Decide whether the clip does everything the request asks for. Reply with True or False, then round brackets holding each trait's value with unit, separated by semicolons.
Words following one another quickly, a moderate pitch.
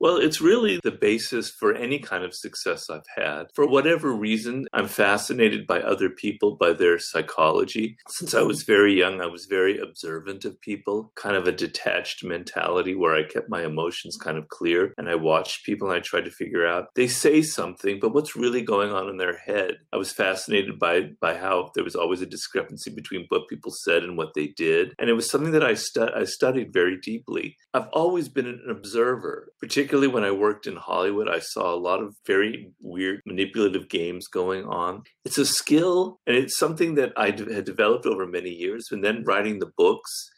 True (210 wpm; 145 Hz)